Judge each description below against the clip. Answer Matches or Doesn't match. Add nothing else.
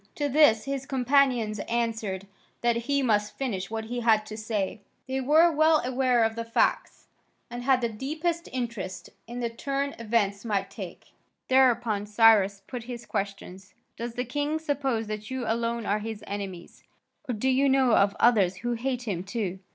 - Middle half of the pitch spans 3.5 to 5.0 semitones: Matches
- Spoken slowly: Doesn't match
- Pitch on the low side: Doesn't match